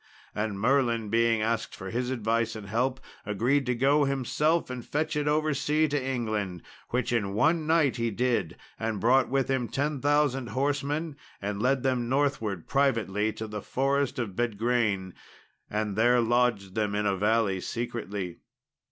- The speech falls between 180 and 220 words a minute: No, average, 160 wpm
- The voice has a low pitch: Yes, low, 120 Hz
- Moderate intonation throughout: Yes, average, 4.2 semitones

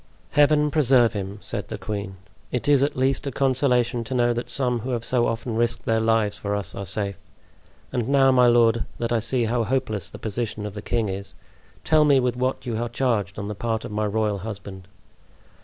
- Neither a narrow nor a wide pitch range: Yes, average, 3.4 semitones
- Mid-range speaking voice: No, low, 115 Hz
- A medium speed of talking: No, fast, 215 wpm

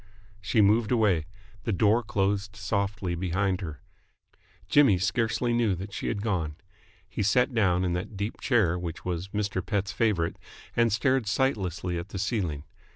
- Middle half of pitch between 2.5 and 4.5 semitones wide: Yes, average, 3.5 semitones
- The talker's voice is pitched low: Yes, low, 100 Hz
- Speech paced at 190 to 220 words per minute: No, average, 155 wpm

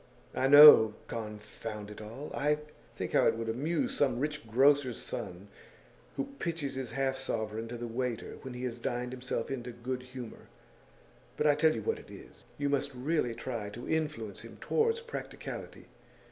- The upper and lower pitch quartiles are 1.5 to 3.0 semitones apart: No, average, 4.0 semitones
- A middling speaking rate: Yes, average, 170 wpm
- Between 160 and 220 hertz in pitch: No, low, 125 Hz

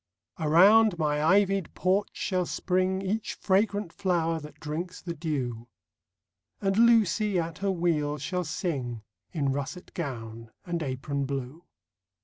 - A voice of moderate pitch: Yes, medium, 170 Hz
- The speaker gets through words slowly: Yes, slow, 130 wpm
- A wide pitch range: No, average, 4.6 semitones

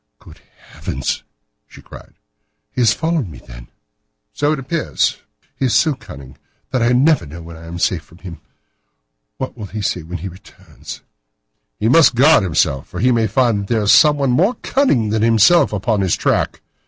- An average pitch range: No, wide, 7.2 semitones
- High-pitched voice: No, low, 110 Hz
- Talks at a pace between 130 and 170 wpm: No, average, 185 wpm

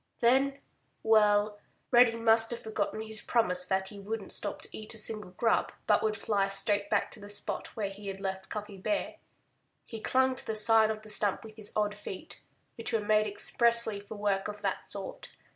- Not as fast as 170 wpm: No, average, 195 wpm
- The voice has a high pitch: Yes, high, 215 Hz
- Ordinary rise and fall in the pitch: No, narrow, 1.8 semitones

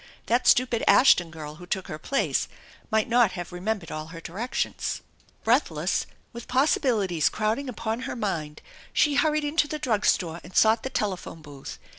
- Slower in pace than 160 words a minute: No, average, 165 wpm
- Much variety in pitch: Yes, wide, 6.5 semitones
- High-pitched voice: Yes, high, 215 Hz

